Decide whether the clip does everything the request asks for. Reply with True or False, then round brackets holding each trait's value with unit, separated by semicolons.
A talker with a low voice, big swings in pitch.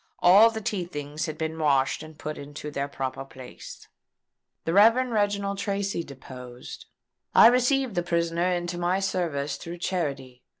False (170 Hz; 5.7 semitones)